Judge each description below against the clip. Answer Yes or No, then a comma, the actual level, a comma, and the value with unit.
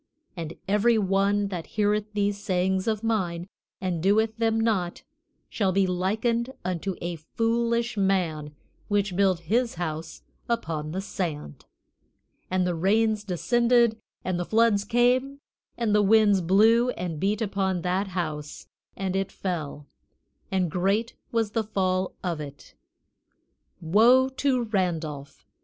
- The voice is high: Yes, high, 195 Hz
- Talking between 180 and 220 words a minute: No, slow, 135 wpm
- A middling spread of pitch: Yes, average, 4.0 semitones